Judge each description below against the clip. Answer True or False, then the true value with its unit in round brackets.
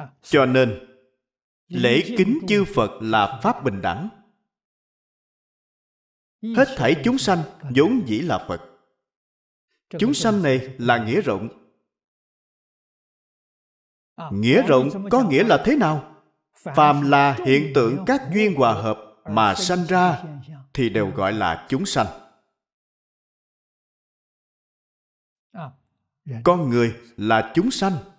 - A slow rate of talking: True (115 wpm)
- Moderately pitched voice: True (145 Hz)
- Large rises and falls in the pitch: True (8.3 semitones)